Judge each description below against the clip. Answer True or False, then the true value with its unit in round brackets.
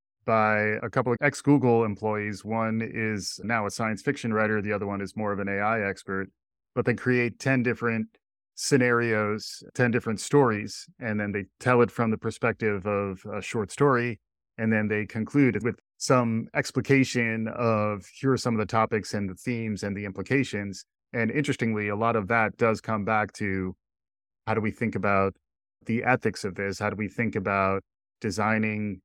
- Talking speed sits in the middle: True (185 wpm)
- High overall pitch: False (110 Hz)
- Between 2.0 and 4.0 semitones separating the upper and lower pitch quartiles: True (2.5 semitones)